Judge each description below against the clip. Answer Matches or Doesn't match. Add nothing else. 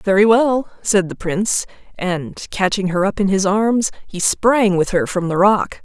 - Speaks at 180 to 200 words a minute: Matches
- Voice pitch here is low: Doesn't match